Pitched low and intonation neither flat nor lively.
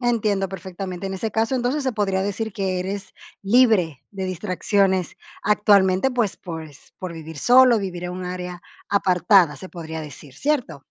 No: high, 190 Hz; average, 3.1 semitones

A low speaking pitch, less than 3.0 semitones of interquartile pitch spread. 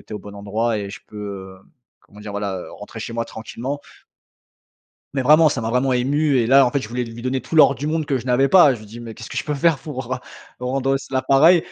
No: low, 125 Hz; average, 3.9 semitones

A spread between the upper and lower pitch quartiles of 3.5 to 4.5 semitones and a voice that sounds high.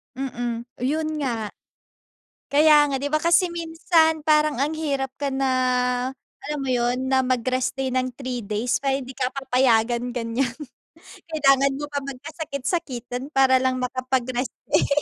No: average, 2.8 semitones; very high, 265 Hz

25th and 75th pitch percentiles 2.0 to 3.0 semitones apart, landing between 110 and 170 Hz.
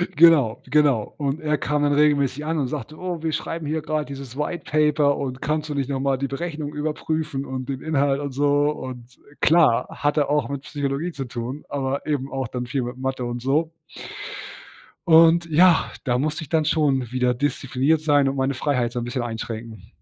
Yes: narrow, 2.6 semitones; medium, 140 Hz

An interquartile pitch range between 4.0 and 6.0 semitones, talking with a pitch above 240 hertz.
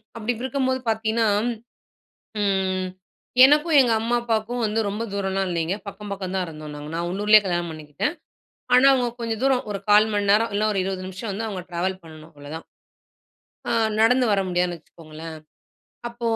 No: average, 4.4 semitones; high, 200 Hz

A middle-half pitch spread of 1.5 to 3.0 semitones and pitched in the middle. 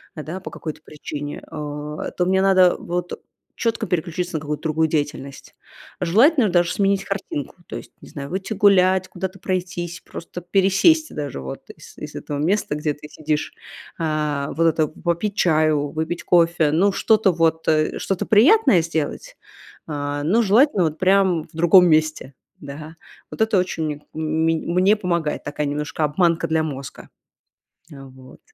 No: average, 3.9 semitones; medium, 165 Hz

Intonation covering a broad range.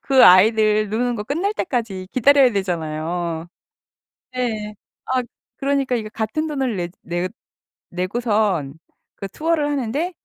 Yes: wide, 6.3 semitones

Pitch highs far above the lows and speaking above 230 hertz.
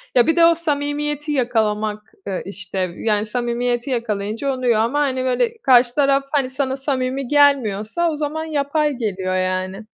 No: average, 5.0 semitones; very high, 255 Hz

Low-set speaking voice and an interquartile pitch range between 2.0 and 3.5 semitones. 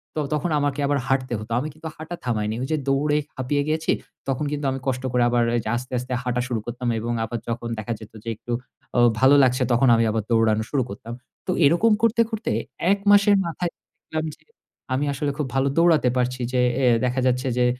No: low, 130 Hz; average, 3.9 semitones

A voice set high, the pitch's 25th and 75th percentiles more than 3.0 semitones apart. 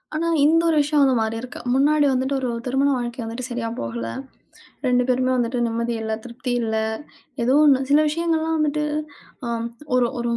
Yes: very high, 255 Hz; average, 3.7 semitones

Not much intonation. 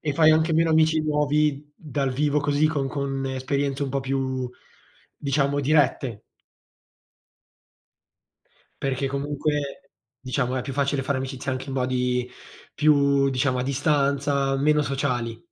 Yes: narrow, 1.9 semitones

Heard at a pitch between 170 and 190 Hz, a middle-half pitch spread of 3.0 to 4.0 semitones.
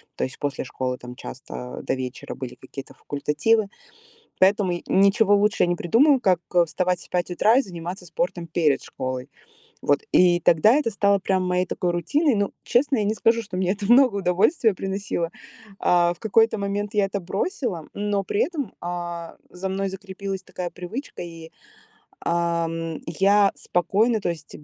Yes: medium, 185 Hz; average, 3.4 semitones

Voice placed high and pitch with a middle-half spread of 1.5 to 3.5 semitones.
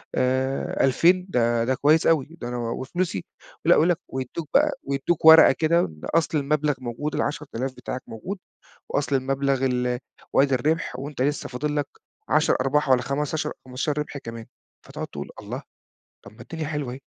No: medium, 140 Hz; average, 3.1 semitones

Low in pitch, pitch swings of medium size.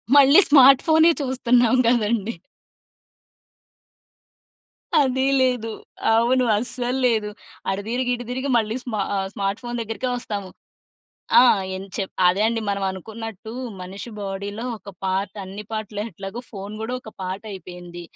No: high, 220 Hz; average, 3.9 semitones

